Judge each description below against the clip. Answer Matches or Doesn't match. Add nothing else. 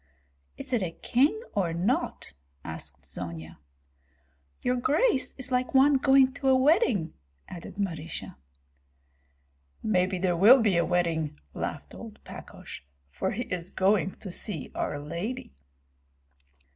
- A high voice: Matches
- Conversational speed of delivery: Doesn't match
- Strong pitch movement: Matches